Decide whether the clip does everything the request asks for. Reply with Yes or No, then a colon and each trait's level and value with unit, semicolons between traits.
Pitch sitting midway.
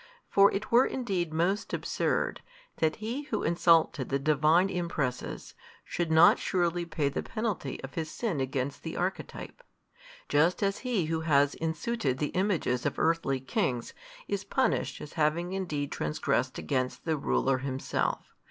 Yes: medium, 160 Hz